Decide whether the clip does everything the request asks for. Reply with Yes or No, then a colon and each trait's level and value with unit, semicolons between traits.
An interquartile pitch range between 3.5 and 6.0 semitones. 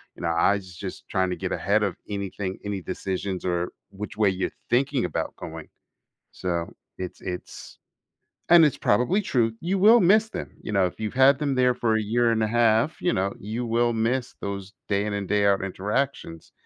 Yes: average, 4.5 semitones